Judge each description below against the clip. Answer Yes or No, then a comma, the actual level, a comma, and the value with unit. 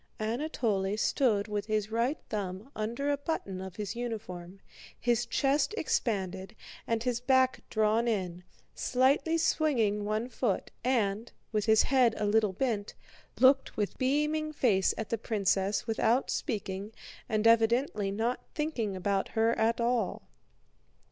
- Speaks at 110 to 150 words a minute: Yes, slow, 135 wpm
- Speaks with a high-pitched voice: Yes, high, 225 Hz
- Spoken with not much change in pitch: No, average, 3.8 semitones